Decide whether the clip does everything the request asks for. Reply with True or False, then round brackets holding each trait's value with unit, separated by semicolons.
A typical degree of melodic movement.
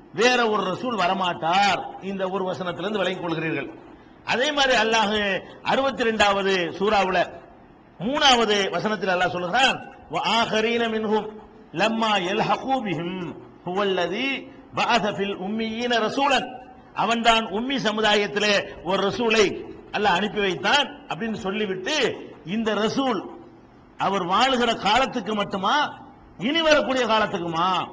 True (3.8 semitones)